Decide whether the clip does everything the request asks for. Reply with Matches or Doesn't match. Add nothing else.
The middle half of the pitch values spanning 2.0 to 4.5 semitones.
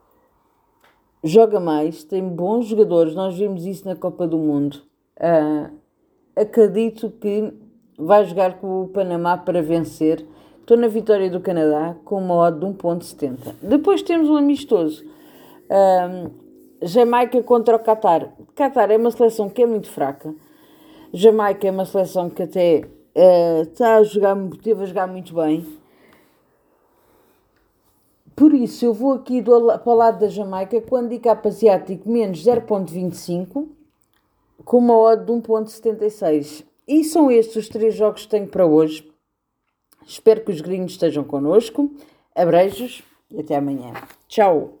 Doesn't match